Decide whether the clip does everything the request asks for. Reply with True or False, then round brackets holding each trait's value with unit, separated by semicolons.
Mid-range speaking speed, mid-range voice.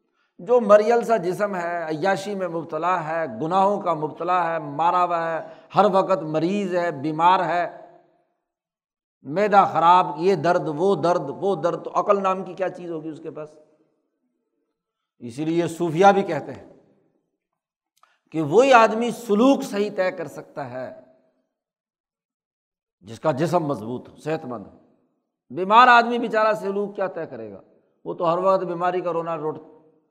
True (155 wpm; 175 Hz)